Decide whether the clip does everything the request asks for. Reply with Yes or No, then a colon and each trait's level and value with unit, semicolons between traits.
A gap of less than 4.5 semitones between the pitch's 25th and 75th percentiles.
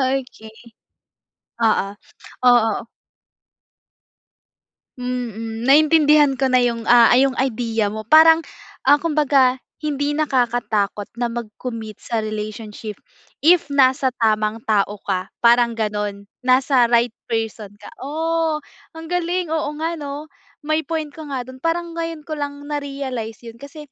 No: average, 5.0 semitones